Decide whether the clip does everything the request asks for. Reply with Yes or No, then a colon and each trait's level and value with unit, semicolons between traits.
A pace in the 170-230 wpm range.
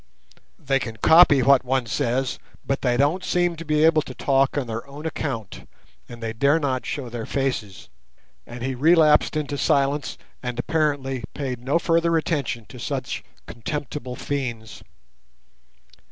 No: average, 155 wpm